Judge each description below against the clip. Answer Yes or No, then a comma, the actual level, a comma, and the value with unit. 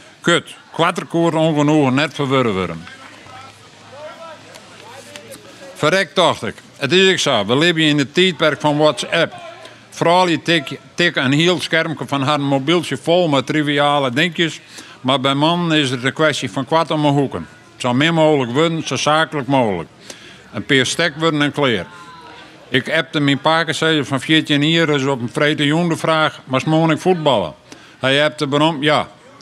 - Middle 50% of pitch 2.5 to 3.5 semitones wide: Yes, average, 2.8 semitones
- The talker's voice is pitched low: No, medium, 150 Hz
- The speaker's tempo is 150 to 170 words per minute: Yes, average, 165 wpm